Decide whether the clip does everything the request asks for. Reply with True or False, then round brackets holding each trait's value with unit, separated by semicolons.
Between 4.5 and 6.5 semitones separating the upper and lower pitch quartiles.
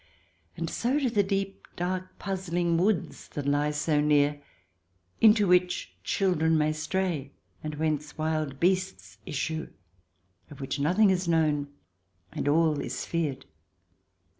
False (3.9 semitones)